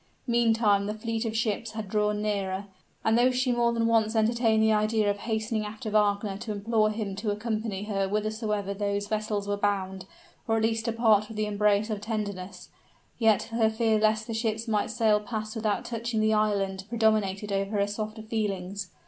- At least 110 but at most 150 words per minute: No, average, 190 wpm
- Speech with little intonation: Yes, narrow, 1.5 semitones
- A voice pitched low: No, high, 215 Hz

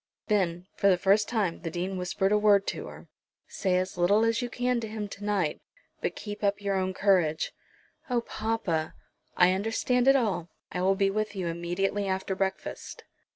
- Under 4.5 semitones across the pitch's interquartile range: Yes, average, 2.7 semitones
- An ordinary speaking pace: Yes, average, 185 wpm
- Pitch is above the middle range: Yes, high, 195 Hz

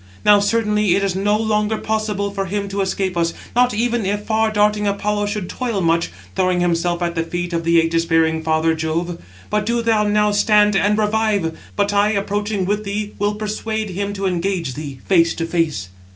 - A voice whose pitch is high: Yes, high, 200 Hz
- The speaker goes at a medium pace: Yes, average, 195 wpm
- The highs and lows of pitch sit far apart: No, average, 3.5 semitones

